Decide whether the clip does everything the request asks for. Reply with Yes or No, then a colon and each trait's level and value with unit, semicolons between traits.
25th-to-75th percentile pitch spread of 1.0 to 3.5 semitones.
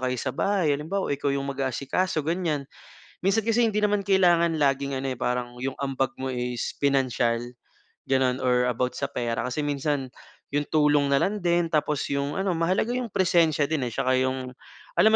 No: average, 4.8 semitones